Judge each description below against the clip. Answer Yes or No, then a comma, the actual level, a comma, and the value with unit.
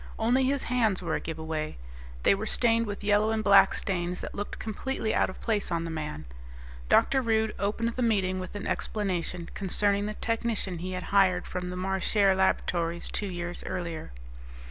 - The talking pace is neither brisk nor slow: Yes, average, 180 wpm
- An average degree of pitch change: Yes, average, 3.6 semitones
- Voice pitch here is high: Yes, high, 195 Hz